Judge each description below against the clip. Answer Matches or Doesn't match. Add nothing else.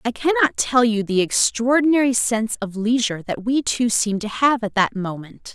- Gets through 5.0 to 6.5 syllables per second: Matches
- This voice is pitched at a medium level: Doesn't match